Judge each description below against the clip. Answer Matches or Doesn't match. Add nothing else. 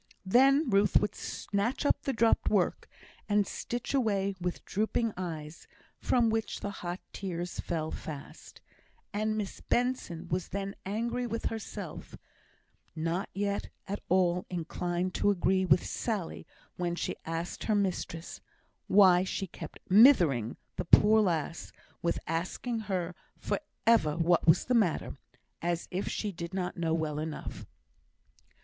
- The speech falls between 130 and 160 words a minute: Matches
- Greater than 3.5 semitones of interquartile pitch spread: Matches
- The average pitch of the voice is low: Doesn't match